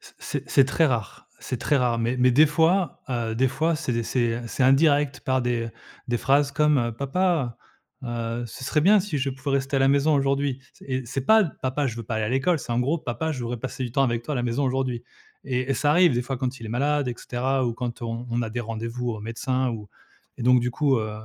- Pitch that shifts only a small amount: No, average, 3.0 semitones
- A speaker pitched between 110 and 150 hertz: Yes, low, 130 Hz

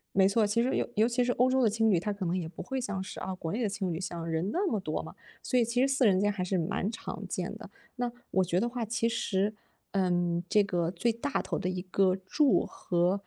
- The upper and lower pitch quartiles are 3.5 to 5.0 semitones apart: Yes, average, 4.3 semitones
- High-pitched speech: Yes, high, 200 Hz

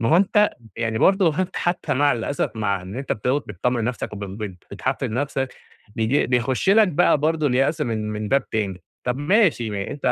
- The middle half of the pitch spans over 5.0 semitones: Yes, wide, 5.6 semitones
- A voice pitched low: Yes, low, 125 Hz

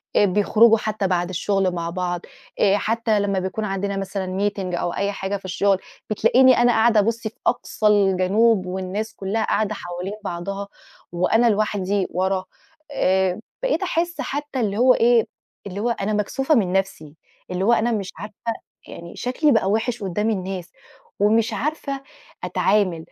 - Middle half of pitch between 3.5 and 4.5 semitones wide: No, average, 3.1 semitones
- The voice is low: No, high, 200 Hz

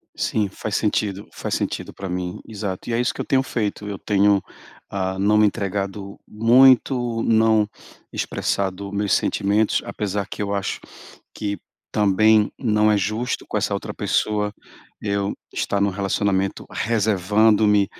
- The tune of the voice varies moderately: No, narrow, 1.7 semitones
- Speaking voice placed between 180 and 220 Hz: No, low, 105 Hz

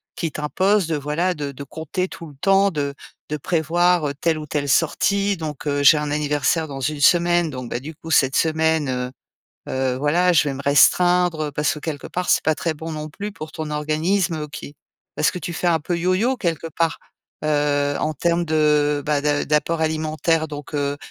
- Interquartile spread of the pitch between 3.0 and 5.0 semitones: No, narrow, 2.6 semitones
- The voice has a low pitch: No, medium, 155 Hz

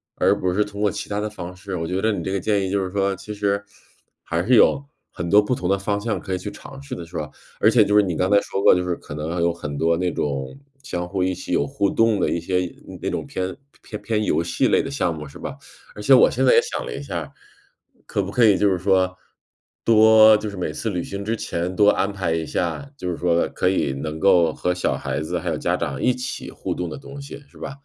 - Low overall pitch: Yes, very low, 95 Hz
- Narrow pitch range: No, average, 3.4 semitones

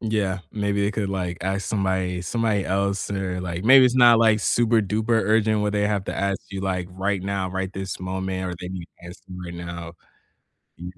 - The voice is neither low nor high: No, very low, 95 Hz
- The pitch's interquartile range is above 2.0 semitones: Yes, narrow, 2.4 semitones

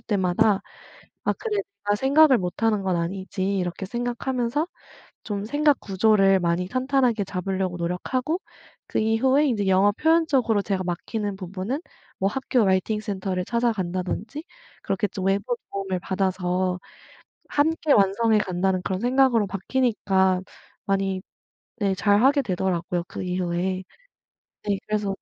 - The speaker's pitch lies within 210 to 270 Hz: No, high, 200 Hz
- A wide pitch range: No, average, 4.3 semitones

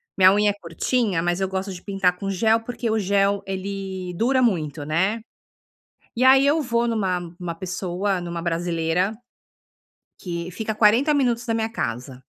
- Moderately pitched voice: No, high, 195 Hz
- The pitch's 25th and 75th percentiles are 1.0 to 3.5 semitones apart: No, average, 4.3 semitones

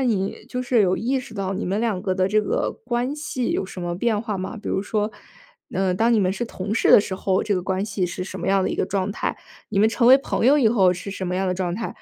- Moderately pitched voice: No, high, 200 Hz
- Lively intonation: No, average, 3.7 semitones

